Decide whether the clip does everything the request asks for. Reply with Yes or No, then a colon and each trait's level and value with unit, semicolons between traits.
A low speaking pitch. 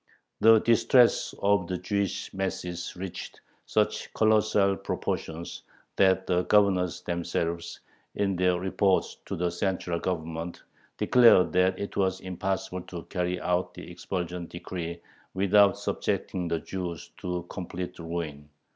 Yes: very low, 90 Hz